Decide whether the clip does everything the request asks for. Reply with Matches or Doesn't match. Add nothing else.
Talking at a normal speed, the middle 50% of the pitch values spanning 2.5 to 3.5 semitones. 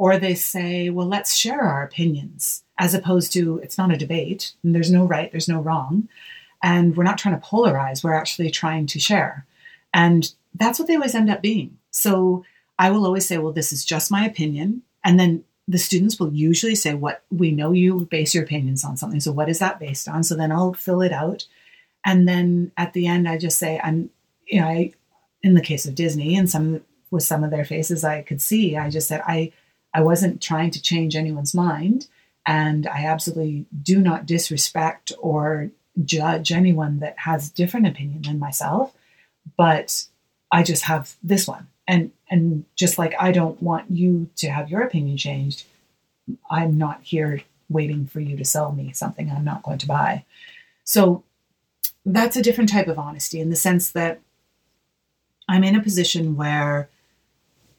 Matches